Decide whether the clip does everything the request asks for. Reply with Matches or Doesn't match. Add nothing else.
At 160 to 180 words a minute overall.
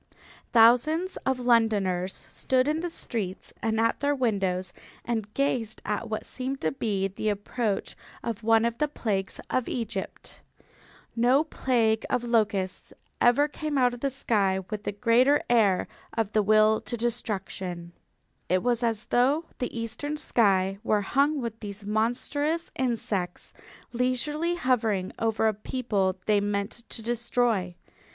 Doesn't match